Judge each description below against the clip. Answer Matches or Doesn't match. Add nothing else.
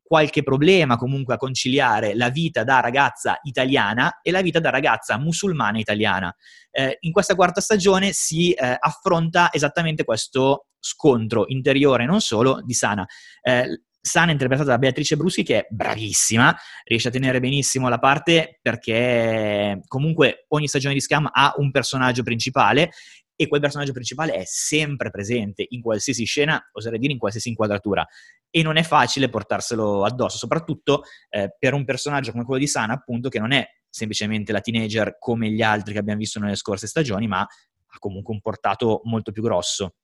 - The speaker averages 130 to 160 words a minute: Doesn't match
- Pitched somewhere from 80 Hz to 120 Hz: Doesn't match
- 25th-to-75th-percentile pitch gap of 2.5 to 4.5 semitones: Doesn't match